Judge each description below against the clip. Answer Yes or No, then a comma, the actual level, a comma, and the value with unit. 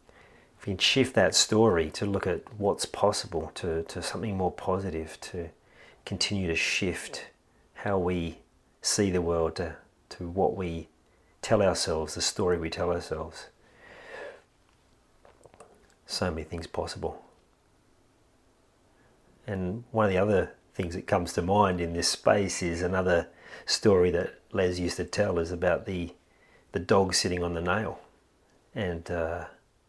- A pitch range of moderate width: No, narrow, 1.8 semitones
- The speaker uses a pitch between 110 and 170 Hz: No, very low, 90 Hz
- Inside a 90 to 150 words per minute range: Yes, average, 140 wpm